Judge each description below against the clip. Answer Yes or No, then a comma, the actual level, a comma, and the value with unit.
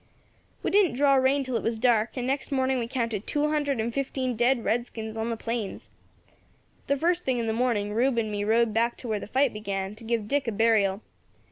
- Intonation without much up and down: No, average, 3.2 semitones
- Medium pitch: No, high, 235 Hz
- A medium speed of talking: No, fast, 225 wpm